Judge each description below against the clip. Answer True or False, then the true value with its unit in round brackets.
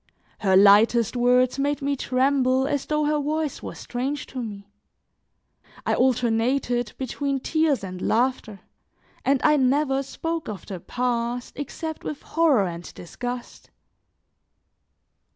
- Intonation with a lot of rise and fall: False (3.4 semitones)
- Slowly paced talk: True (125 wpm)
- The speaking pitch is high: True (255 Hz)